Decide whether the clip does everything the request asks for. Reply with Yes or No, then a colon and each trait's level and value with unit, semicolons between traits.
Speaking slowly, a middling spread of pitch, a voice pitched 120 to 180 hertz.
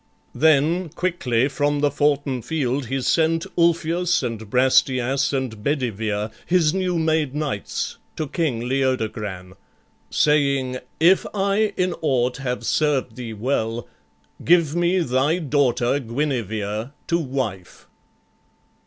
Yes: slow, 115 wpm; average, 4.7 semitones; medium, 140 Hz